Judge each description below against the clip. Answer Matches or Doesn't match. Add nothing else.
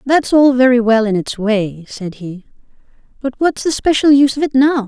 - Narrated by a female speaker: Matches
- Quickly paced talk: Matches